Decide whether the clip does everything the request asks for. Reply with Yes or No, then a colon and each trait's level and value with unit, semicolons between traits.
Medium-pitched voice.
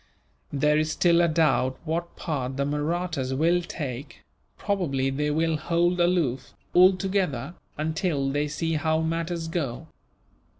Yes: medium, 160 Hz